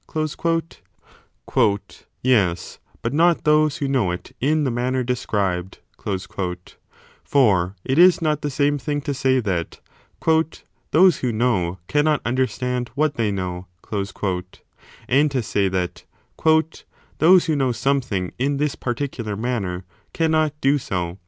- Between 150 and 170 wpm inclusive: No, slow, 135 wpm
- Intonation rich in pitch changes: Yes, wide, 6.4 semitones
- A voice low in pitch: Yes, low, 130 Hz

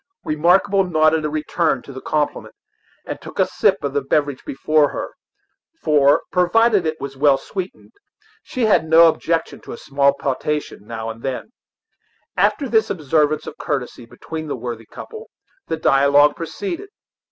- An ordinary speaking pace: Yes, average, 155 wpm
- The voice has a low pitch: No, medium, 155 Hz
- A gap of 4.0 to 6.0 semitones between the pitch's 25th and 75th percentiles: No, average, 3.5 semitones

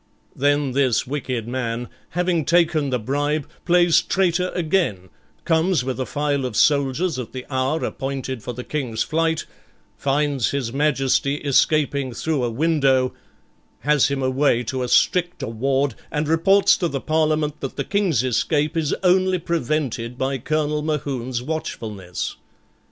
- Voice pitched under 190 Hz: Yes, medium, 140 Hz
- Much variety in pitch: No, average, 3.6 semitones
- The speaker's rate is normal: Yes, average, 145 wpm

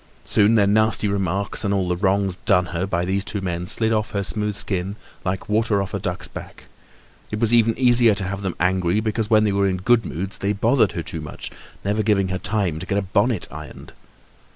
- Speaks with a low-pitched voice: Yes, low, 100 Hz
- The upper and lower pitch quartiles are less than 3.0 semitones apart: Yes, narrow, 2.6 semitones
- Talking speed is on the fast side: Yes, fast, 225 wpm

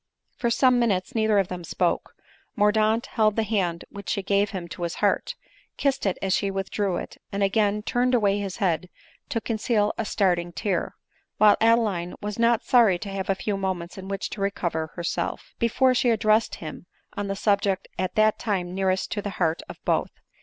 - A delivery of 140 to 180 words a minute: No, average, 195 wpm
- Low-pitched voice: No, high, 200 Hz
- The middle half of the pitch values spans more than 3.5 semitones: No, average, 2.7 semitones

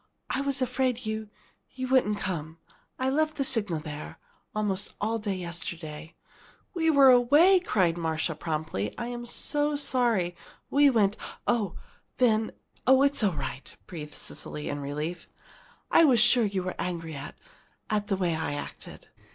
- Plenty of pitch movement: Yes, wide, 7.6 semitones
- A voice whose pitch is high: Yes, high, 210 Hz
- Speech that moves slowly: No, average, 160 wpm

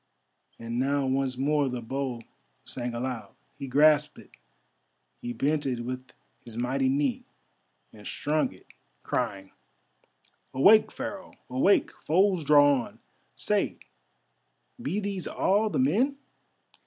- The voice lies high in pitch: No, low, 135 Hz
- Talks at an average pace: No, slow, 120 wpm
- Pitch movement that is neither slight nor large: Yes, average, 3.8 semitones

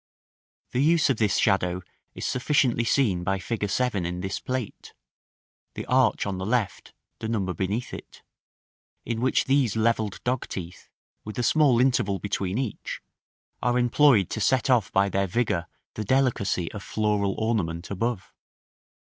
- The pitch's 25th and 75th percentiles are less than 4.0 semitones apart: No, average, 4.4 semitones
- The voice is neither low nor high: No, low, 110 Hz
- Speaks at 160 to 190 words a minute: No, average, 150 wpm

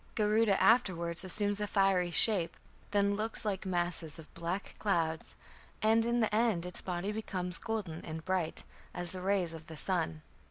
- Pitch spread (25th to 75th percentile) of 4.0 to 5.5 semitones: No, average, 3.6 semitones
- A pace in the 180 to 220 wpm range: No, average, 165 wpm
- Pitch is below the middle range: No, high, 190 Hz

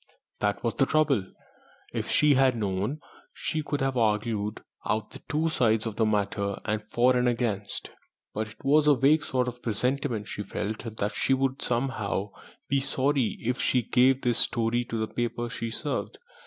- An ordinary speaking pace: Yes, average, 180 wpm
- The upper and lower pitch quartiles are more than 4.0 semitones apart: No, average, 3.7 semitones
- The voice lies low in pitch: Yes, low, 120 Hz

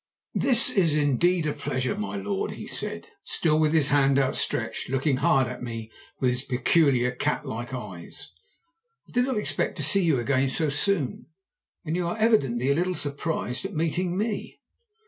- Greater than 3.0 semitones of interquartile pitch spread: Yes, average, 5.2 semitones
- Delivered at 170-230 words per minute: Yes, average, 180 wpm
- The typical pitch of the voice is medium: Yes, medium, 145 Hz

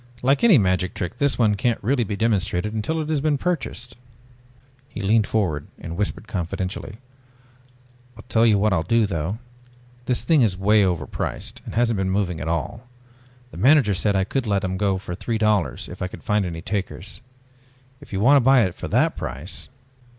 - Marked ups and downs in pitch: No, average, 4.2 semitones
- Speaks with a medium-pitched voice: No, low, 105 Hz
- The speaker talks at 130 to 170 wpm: No, average, 195 wpm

